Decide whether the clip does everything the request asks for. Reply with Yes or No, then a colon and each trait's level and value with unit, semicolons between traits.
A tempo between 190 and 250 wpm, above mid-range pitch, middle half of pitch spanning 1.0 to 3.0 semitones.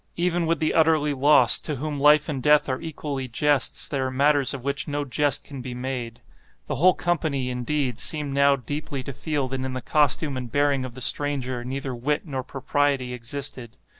No: average, 195 wpm; medium, 140 Hz; narrow, 2.4 semitones